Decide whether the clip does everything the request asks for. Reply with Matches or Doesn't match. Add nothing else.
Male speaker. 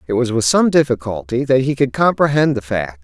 Matches